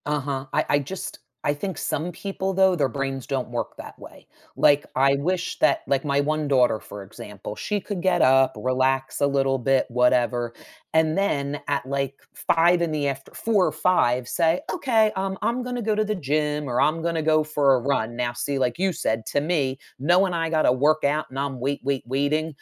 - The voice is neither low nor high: Yes, medium, 145 Hz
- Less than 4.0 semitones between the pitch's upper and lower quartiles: No, average, 4.3 semitones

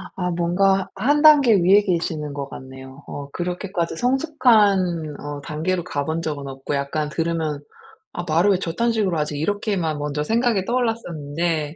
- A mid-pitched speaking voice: Yes, medium, 170 Hz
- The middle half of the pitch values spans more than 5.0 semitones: Yes, wide, 5.4 semitones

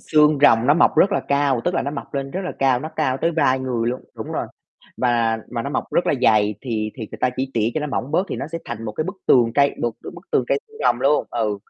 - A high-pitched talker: No, low, 130 Hz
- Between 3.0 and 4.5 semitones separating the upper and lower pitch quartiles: Yes, average, 4.1 semitones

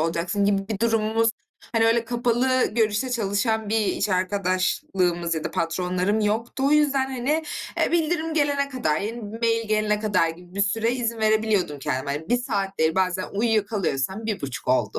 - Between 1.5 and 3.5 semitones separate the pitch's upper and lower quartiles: No, average, 4.1 semitones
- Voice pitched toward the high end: Yes, high, 215 Hz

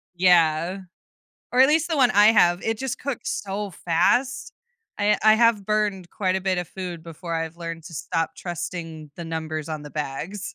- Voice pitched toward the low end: No, medium, 180 Hz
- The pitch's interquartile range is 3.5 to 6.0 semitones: Yes, average, 4.3 semitones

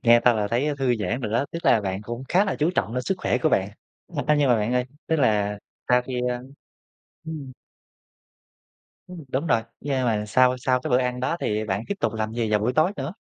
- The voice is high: No, low, 125 Hz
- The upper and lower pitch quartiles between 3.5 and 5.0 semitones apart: Yes, average, 3.9 semitones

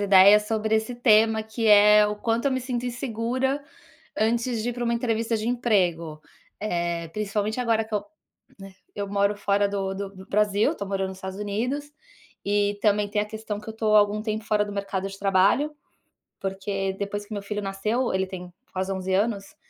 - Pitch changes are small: Yes, narrow, 2.3 semitones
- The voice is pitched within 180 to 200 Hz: No, high, 210 Hz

